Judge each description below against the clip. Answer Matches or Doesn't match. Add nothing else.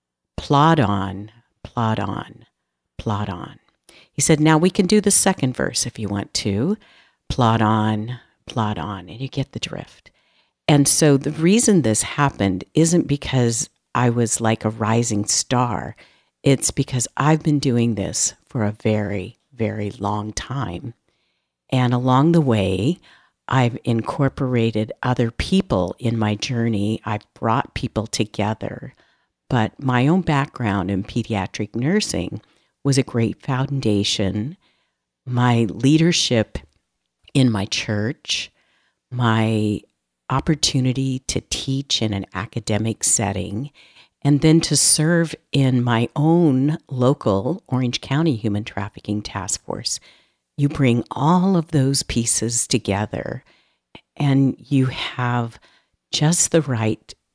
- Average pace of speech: Doesn't match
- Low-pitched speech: Matches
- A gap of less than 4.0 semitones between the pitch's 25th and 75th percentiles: Doesn't match